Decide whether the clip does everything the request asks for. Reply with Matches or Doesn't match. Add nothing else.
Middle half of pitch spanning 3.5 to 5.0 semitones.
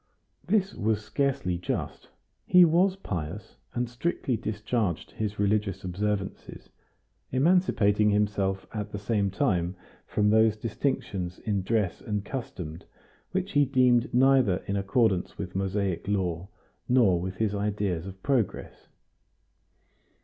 Matches